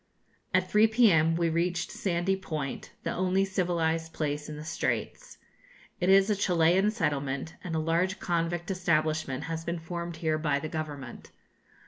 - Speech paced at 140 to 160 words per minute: Yes, average, 155 wpm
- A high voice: No, medium, 165 Hz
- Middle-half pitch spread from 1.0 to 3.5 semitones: Yes, average, 2.7 semitones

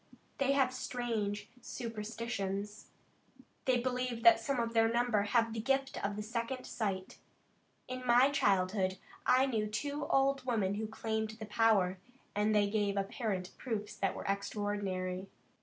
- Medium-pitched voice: No, high, 220 Hz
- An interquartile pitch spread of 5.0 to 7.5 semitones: No, average, 3.5 semitones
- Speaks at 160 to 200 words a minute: No, average, 140 wpm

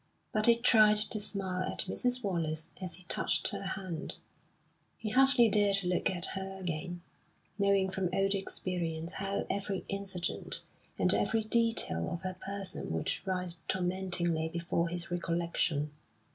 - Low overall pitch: No, high, 190 Hz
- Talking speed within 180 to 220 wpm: No, average, 145 wpm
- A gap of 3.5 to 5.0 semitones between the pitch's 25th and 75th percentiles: No, narrow, 2.5 semitones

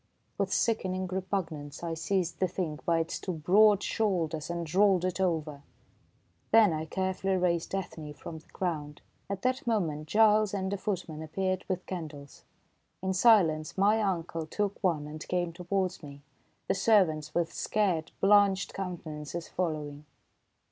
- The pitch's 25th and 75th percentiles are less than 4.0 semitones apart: Yes, average, 3.5 semitones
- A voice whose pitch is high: No, medium, 180 Hz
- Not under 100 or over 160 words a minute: Yes, average, 150 wpm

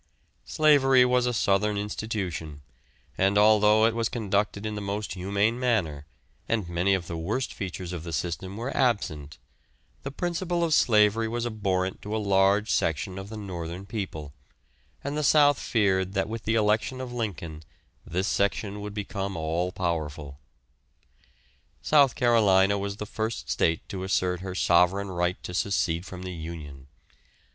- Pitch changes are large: No, average, 3.8 semitones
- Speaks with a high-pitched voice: No, low, 100 Hz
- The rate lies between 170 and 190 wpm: No, average, 155 wpm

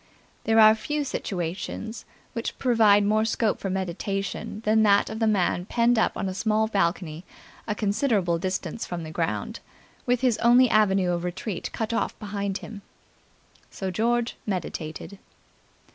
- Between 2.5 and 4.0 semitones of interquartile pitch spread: Yes, average, 3.2 semitones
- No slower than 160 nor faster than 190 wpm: No, average, 150 wpm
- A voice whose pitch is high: Yes, high, 205 Hz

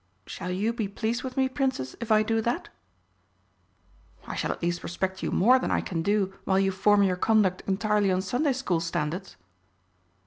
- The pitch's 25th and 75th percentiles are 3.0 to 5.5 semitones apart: Yes, average, 3.8 semitones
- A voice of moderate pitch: No, high, 200 Hz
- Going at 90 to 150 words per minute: No, average, 185 wpm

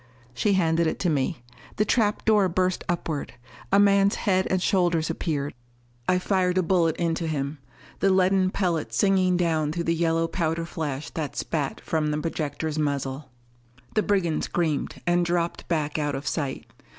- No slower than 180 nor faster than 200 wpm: No, average, 165 wpm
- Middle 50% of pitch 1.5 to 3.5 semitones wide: Yes, average, 3.2 semitones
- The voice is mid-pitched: Yes, medium, 165 Hz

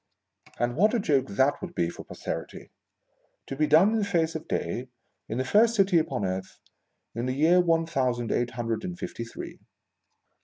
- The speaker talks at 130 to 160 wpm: No, average, 190 wpm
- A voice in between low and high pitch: Yes, medium, 150 Hz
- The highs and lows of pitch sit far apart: Yes, wide, 6.7 semitones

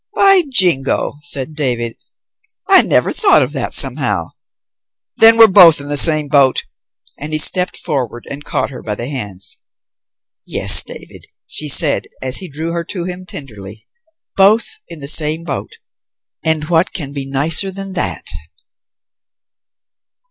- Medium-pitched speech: Yes, medium, 150 Hz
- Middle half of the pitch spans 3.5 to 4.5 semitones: No, average, 4.9 semitones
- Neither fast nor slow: Yes, average, 150 wpm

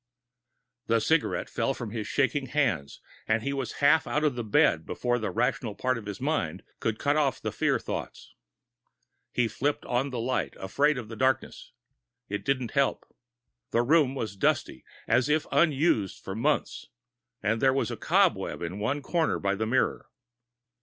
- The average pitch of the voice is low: Yes, low, 125 Hz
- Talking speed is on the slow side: No, average, 175 wpm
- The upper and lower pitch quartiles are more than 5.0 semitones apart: No, average, 4.2 semitones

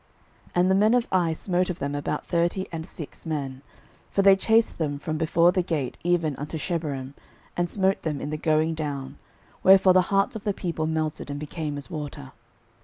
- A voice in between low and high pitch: Yes, medium, 160 Hz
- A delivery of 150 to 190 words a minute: No, average, 200 wpm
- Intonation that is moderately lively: Yes, average, 3.8 semitones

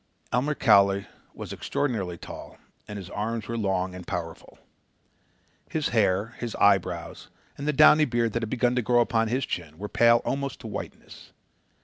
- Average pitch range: Yes, average, 3.9 semitones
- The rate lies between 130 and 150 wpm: No, average, 165 wpm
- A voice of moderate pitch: No, low, 115 Hz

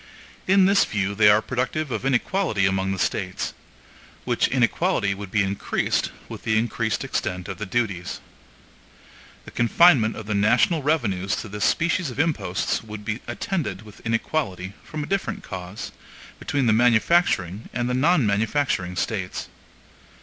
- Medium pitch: No, low, 110 Hz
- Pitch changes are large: Yes, wide, 6.0 semitones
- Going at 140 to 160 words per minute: Yes, average, 150 wpm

